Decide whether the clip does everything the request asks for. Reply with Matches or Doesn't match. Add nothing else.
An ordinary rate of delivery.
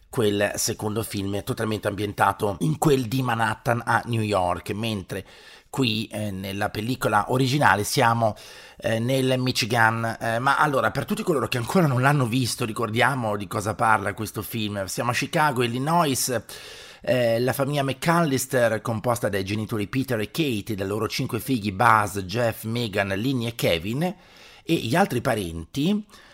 Matches